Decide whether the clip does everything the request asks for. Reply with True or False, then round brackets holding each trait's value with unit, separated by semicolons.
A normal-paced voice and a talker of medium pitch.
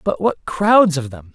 False (225 wpm; 165 Hz)